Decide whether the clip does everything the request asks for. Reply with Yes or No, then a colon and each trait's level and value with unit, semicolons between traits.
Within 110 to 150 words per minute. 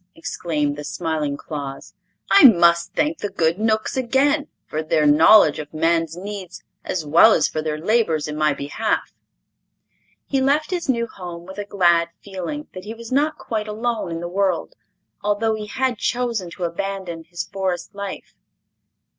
No: average, 165 wpm